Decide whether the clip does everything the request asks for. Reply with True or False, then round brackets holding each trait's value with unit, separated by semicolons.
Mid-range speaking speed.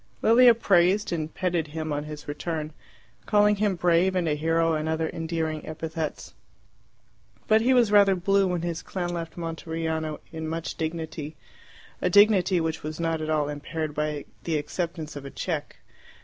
True (165 wpm)